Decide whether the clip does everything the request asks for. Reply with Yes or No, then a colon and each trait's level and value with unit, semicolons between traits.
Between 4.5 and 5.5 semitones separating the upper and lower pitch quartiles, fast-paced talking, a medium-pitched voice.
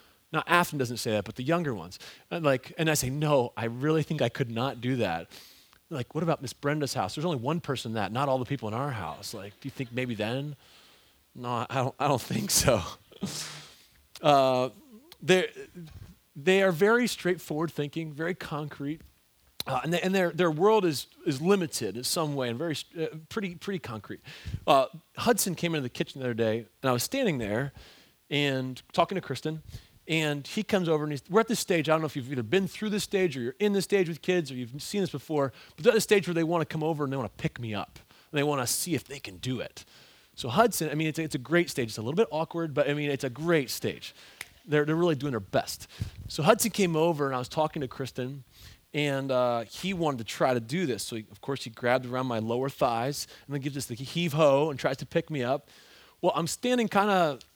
Yes: average, 5.0 semitones; fast, 245 wpm; medium, 145 Hz